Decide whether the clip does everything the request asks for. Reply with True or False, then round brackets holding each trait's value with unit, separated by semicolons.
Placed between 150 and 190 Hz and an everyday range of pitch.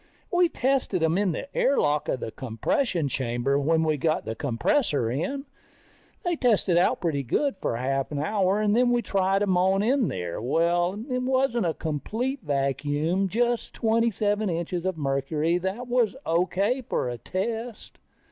False (185 Hz; 8.0 semitones)